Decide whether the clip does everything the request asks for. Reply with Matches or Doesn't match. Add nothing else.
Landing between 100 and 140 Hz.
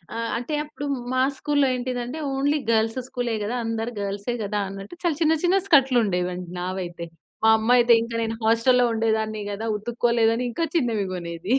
Doesn't match